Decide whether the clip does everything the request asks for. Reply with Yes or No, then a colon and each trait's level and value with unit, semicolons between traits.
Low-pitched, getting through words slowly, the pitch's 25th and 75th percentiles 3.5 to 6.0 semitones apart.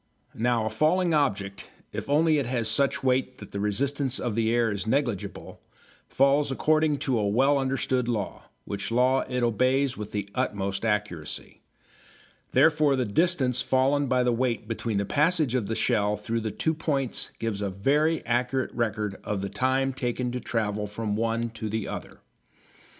No: low, 120 Hz; average, 170 wpm; average, 4.3 semitones